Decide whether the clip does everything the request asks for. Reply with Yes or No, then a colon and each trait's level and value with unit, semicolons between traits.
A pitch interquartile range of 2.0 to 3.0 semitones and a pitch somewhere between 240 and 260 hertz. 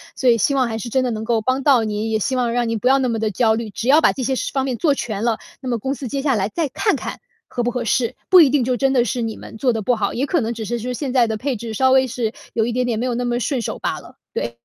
Yes: average, 2.7 semitones; high, 245 Hz